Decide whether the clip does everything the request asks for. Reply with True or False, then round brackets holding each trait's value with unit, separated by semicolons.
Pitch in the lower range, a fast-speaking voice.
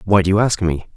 True (95 Hz; 315 wpm)